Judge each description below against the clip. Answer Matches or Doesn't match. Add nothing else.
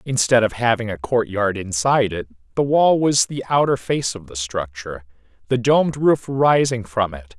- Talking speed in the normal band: Matches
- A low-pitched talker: Matches